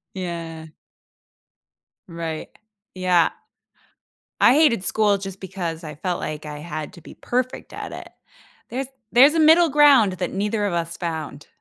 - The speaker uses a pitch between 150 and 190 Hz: Yes, medium, 185 Hz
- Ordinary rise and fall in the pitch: No, wide, 6.0 semitones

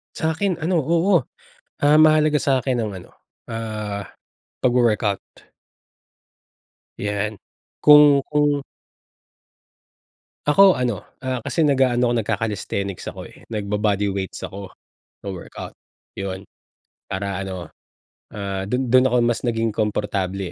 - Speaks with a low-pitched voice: Yes, low, 115 Hz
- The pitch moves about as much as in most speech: No, wide, 5.8 semitones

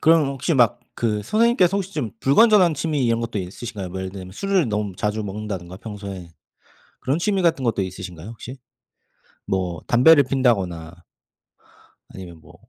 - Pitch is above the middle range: No, low, 115 Hz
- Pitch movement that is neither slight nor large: No, wide, 8.0 semitones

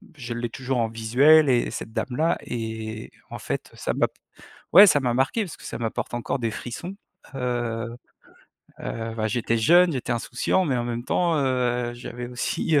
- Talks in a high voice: No, low, 120 Hz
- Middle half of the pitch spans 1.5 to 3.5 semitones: Yes, average, 2.9 semitones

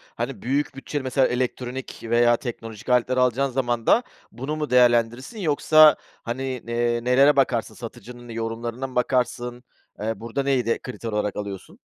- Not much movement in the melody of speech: Yes, narrow, 2.2 semitones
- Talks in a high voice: No, low, 125 Hz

